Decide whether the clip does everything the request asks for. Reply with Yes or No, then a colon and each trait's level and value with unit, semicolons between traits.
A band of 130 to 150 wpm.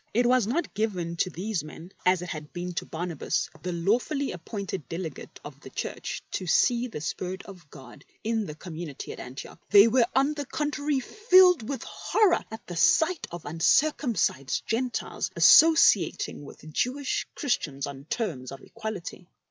No: average, 165 wpm